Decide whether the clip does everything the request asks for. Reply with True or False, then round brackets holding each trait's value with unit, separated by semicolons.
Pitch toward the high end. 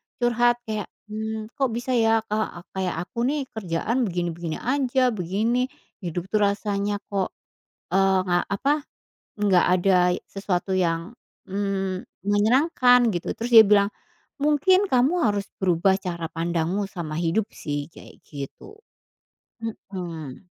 True (200 Hz)